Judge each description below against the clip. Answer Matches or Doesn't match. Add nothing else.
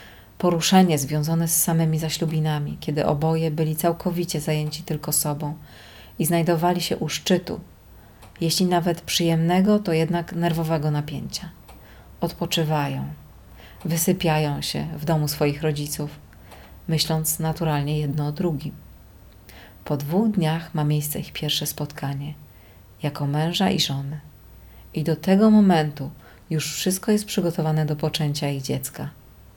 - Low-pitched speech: Doesn't match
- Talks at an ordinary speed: Matches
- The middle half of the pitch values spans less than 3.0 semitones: Matches